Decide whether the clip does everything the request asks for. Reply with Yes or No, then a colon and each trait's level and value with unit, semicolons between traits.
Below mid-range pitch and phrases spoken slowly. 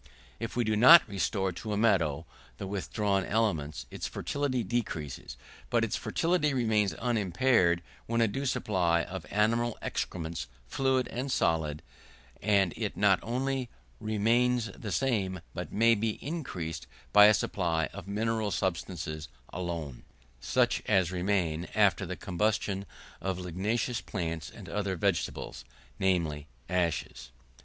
Yes: low, 100 Hz; slow, 130 wpm